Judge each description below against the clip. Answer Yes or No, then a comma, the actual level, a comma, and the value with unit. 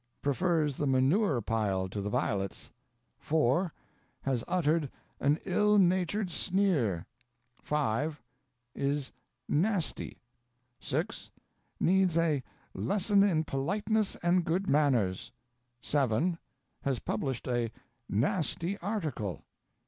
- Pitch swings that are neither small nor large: No, wide, 6.1 semitones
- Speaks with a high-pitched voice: No, medium, 150 Hz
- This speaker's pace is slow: Yes, slow, 95 wpm